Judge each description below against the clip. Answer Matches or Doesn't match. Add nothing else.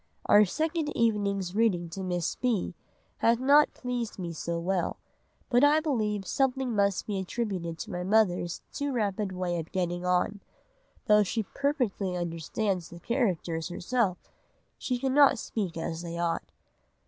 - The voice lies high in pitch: Matches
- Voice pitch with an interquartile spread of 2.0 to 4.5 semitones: Doesn't match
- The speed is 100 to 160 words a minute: Matches